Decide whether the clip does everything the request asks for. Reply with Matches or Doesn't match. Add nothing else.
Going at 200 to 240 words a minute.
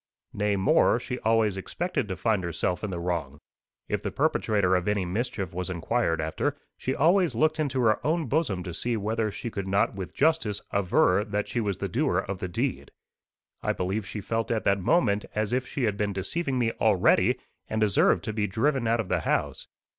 Matches